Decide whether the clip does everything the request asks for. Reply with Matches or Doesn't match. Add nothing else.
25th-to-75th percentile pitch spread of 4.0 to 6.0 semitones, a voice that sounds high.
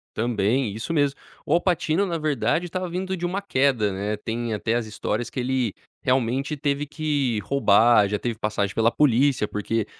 Doesn't match